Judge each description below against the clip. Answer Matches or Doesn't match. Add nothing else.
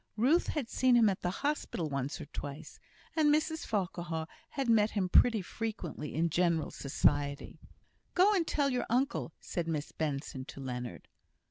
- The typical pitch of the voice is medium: Matches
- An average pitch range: Doesn't match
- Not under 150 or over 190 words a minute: Matches